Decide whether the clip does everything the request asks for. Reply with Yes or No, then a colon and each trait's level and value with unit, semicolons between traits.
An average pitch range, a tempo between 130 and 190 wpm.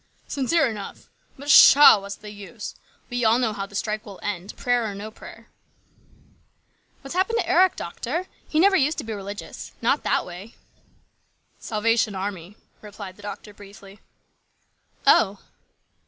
Yes: average, 3.8 semitones; average, 155 wpm